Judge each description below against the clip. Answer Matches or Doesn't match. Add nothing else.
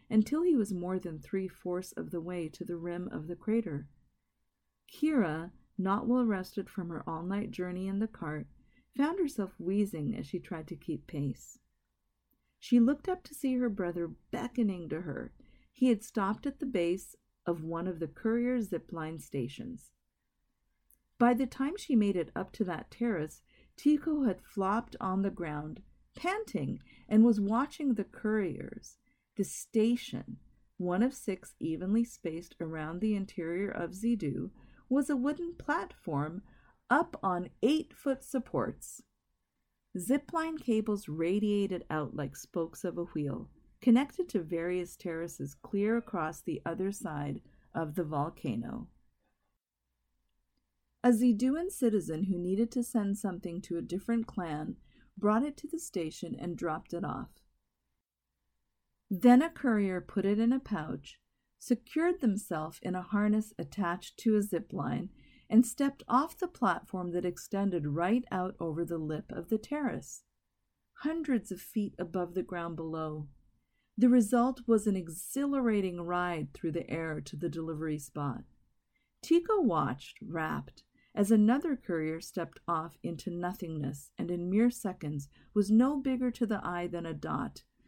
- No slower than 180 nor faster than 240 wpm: Doesn't match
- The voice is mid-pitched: Doesn't match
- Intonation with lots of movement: Matches